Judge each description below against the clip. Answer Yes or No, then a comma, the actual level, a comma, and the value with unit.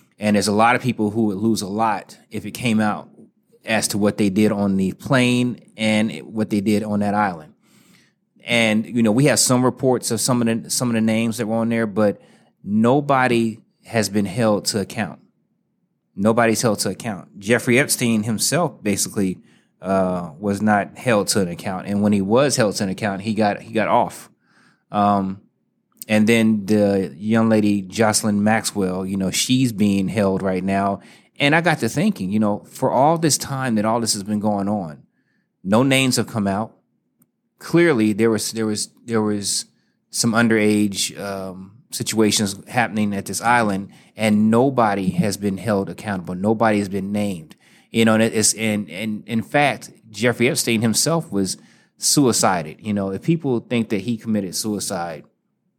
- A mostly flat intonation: Yes, narrow, 2.3 semitones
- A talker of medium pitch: No, low, 110 Hz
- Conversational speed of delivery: Yes, average, 185 wpm